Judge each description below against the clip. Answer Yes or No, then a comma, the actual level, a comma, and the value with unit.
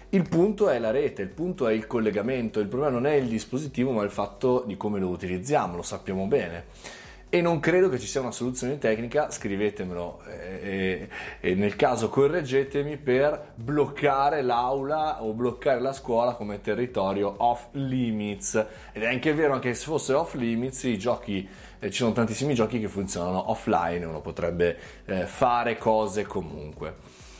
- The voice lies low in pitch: Yes, low, 120 Hz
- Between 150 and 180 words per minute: Yes, average, 165 wpm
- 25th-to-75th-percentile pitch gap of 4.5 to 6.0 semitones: Yes, average, 5.0 semitones